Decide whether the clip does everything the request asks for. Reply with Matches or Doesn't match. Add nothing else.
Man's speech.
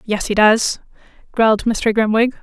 Doesn't match